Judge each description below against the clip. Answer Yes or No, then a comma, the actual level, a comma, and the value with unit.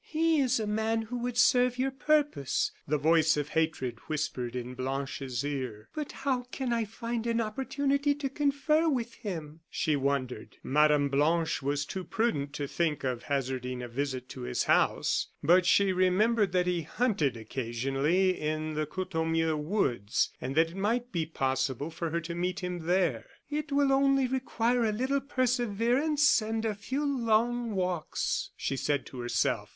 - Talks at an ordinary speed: Yes, average, 165 wpm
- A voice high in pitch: No, medium, 180 Hz